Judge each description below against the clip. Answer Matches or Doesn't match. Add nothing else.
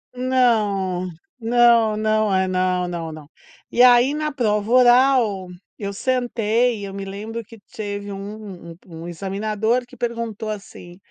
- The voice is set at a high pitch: Matches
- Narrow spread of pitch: Doesn't match